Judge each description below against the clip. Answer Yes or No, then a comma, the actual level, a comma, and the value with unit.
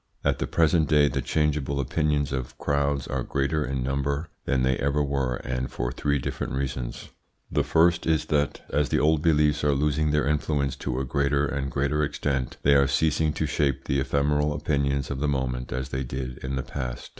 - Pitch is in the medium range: No, very low, 70 Hz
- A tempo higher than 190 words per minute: Yes, average, 200 wpm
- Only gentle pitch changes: Yes, narrow, 2.0 semitones